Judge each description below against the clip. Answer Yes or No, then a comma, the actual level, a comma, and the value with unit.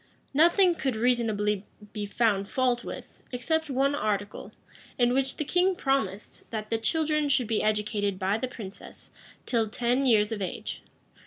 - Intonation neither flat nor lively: Yes, average, 4.5 semitones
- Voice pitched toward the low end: No, high, 240 Hz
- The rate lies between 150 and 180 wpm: Yes, average, 155 wpm